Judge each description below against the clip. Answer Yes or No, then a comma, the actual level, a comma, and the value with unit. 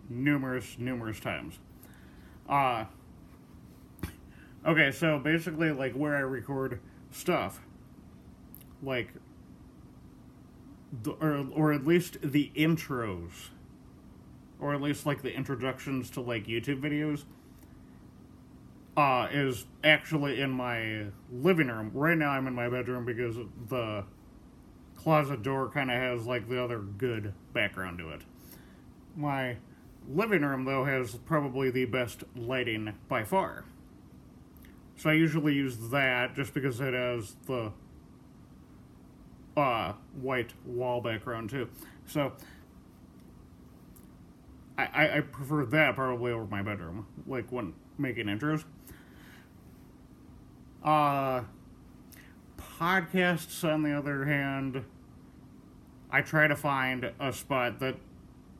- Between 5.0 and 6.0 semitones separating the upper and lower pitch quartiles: Yes, wide, 5.5 semitones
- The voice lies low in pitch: Yes, low, 125 Hz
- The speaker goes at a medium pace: No, slow, 115 wpm